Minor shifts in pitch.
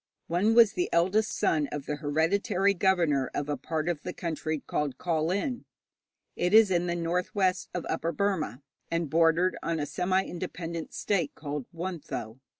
No: average, 3.3 semitones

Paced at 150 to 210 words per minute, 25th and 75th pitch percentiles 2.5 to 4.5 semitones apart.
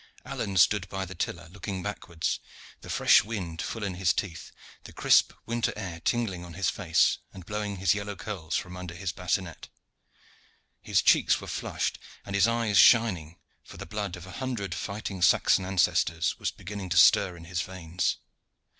Yes: average, 175 wpm; average, 2.9 semitones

